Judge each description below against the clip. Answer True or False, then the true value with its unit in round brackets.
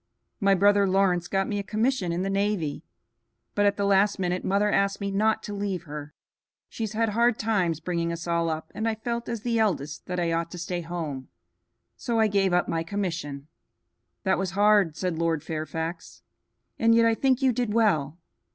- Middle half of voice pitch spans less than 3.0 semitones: False (4.0 semitones)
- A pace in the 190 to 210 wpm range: True (205 wpm)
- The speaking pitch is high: True (195 Hz)